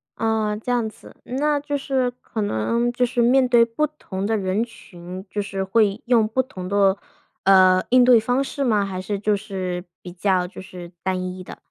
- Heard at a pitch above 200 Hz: Yes, high, 215 Hz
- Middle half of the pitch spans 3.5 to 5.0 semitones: Yes, average, 4.5 semitones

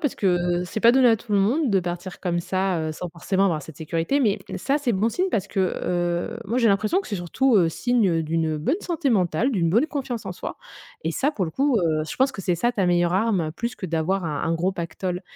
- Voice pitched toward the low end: No, high, 190 Hz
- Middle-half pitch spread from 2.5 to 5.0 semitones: No, wide, 5.5 semitones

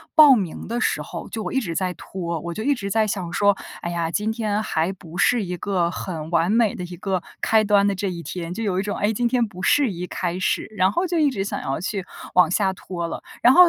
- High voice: Yes, high, 195 Hz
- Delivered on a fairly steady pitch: No, average, 3.8 semitones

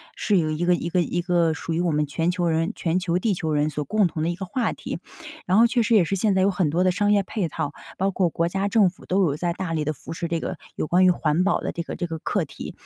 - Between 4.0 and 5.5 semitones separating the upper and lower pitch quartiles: No, average, 2.7 semitones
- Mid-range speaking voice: Yes, medium, 175 Hz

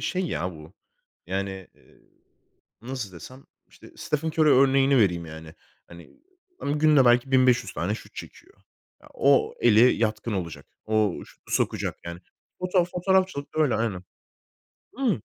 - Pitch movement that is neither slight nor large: No, wide, 7.2 semitones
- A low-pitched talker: Yes, low, 120 Hz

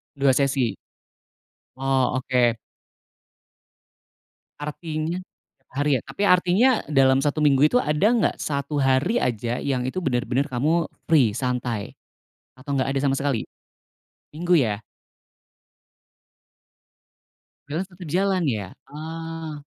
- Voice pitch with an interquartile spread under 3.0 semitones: No, average, 4.1 semitones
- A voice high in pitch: No, medium, 140 Hz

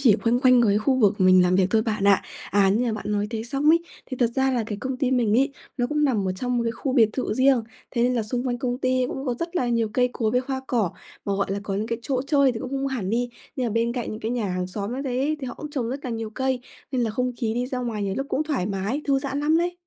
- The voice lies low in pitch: No, high, 245 Hz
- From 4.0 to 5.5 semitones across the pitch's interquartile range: No, average, 3.5 semitones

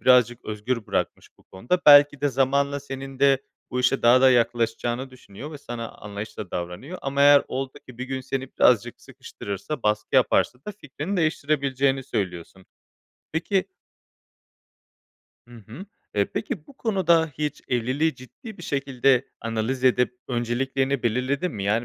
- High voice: No, low, 130 Hz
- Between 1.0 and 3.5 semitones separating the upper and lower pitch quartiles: Yes, average, 3.0 semitones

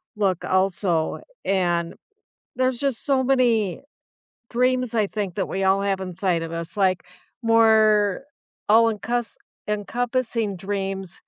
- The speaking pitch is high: Yes, high, 205 Hz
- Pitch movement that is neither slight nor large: Yes, average, 3.4 semitones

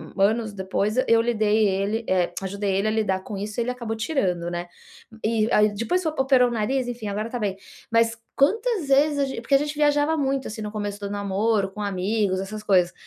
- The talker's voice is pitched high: Yes, high, 215 Hz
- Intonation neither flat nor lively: Yes, average, 3.8 semitones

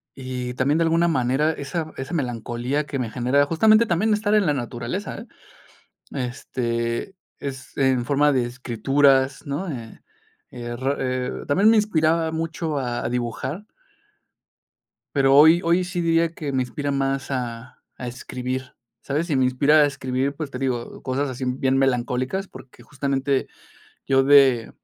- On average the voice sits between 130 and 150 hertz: Yes, low, 135 Hz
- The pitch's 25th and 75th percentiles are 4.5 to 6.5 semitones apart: No, average, 3.7 semitones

